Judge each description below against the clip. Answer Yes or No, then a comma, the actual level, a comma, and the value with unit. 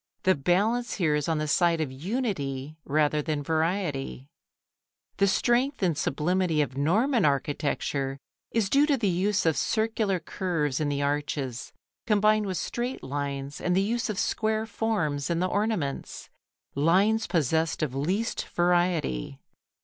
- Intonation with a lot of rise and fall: Yes, wide, 6.3 semitones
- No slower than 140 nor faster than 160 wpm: Yes, average, 145 wpm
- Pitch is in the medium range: Yes, medium, 170 Hz